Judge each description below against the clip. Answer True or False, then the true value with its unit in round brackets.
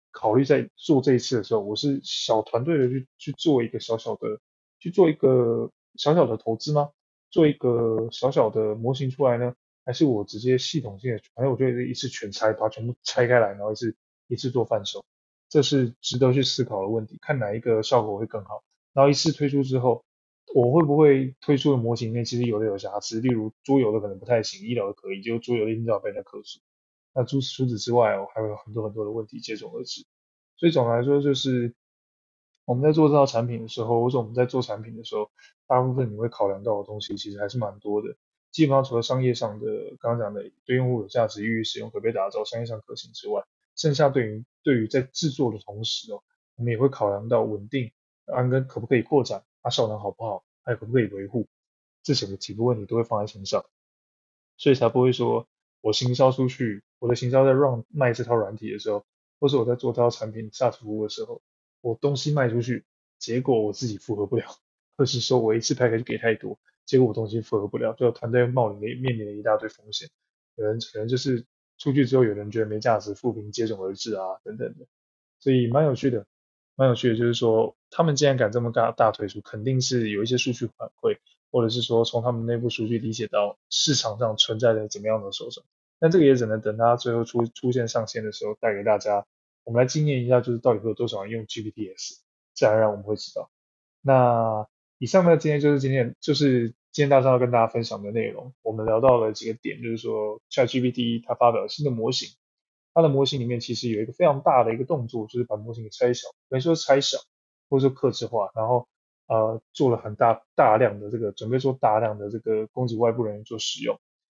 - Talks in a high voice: False (120 Hz)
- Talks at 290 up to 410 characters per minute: True (345 characters per minute)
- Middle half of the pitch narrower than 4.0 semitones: True (3.1 semitones)